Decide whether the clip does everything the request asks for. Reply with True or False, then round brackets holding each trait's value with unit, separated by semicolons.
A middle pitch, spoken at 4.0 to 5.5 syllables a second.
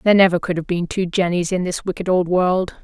False (180 Hz; 5.9 syllables/s)